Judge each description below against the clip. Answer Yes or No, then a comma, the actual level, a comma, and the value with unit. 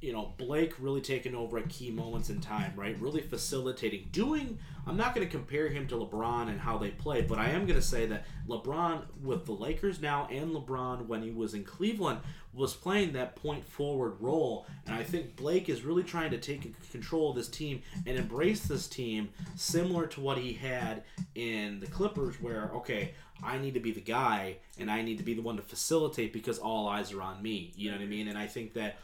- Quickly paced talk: Yes, fast, 225 wpm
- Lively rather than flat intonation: Yes, wide, 6.0 semitones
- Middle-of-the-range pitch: No, low, 130 Hz